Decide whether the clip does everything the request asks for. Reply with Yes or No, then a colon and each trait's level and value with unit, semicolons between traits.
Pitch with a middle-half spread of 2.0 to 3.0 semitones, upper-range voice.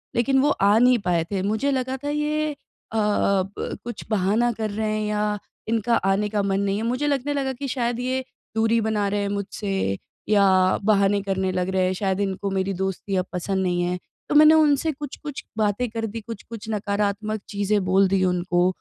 No: average, 3.7 semitones; high, 210 Hz